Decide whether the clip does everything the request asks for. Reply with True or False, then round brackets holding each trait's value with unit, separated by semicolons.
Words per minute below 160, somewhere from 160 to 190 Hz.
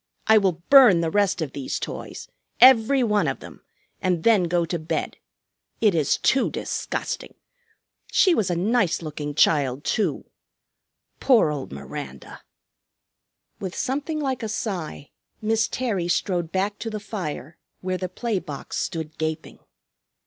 True (145 wpm; 185 Hz)